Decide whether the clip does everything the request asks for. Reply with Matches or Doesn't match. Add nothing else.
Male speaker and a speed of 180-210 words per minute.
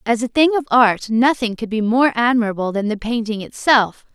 Doesn't match